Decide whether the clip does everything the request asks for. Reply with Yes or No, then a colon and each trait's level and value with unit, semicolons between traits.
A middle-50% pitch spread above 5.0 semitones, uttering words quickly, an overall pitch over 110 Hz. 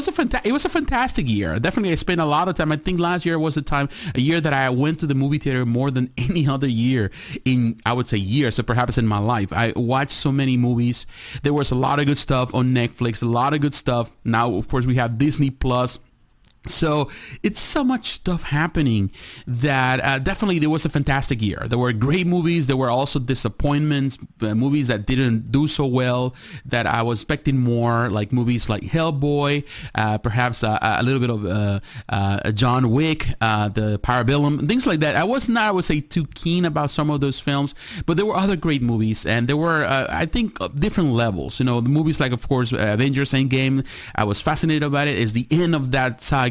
No: average, 4.1 semitones; fast, 225 wpm; low, 135 Hz